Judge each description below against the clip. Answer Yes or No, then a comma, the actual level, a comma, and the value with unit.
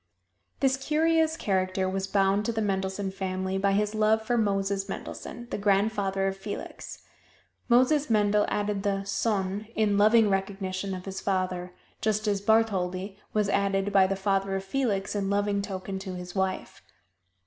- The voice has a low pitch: No, high, 200 Hz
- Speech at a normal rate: Yes, average, 160 wpm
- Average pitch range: No, narrow, 1.7 semitones